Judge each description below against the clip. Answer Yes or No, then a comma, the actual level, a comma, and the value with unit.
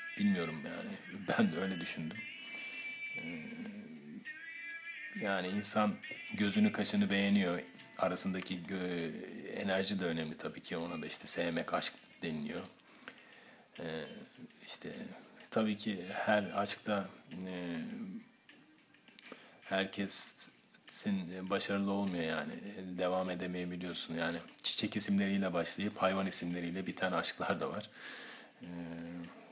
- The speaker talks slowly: Yes, slow, 90 wpm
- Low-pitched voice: Yes, low, 105 Hz